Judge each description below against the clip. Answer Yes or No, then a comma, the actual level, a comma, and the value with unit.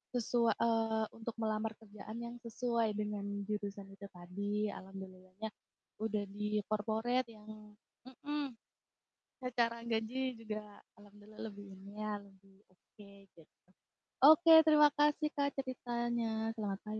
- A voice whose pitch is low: No, high, 220 Hz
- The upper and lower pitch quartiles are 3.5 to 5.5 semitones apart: No, narrow, 2.5 semitones